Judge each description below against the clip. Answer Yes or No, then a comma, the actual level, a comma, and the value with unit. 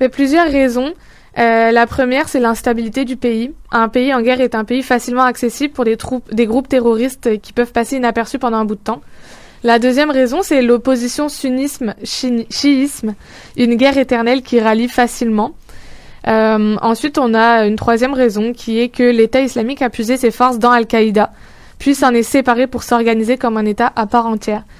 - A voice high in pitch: Yes, high, 245 Hz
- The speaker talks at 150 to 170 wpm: No, average, 185 wpm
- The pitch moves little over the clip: Yes, narrow, 2.2 semitones